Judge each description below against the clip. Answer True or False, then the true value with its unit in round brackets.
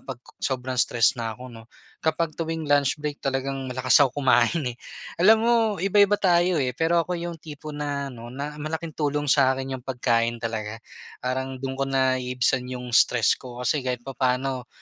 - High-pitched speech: False (135 Hz)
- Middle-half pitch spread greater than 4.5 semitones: False (3.0 semitones)